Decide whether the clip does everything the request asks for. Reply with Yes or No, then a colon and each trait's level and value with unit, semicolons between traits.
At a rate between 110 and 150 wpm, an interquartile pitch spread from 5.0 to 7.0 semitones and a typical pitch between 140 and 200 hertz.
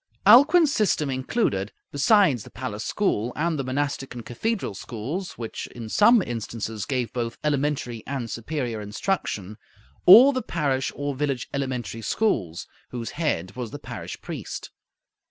No: average, 140 wpm; wide, 5.6 semitones; low, 130 Hz